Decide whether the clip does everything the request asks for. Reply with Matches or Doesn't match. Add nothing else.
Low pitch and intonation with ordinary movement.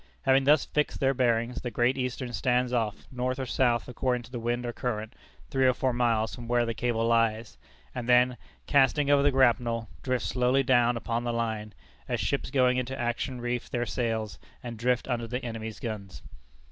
Doesn't match